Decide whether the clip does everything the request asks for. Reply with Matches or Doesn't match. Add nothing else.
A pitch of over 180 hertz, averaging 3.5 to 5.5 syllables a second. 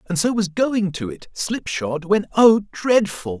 Matches